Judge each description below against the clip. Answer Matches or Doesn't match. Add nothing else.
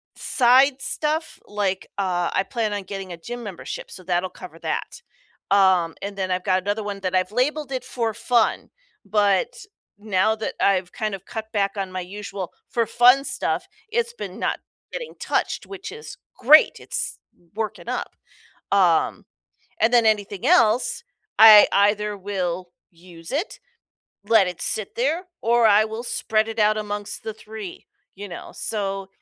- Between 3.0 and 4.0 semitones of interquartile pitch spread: Matches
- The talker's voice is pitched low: Doesn't match